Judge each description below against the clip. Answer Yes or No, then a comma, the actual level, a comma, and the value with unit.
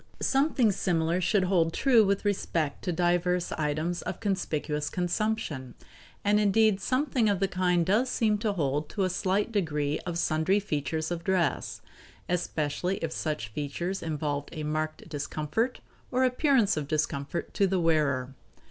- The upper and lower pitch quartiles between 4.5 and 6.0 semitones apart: Yes, average, 4.8 semitones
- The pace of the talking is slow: No, average, 150 wpm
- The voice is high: No, medium, 175 Hz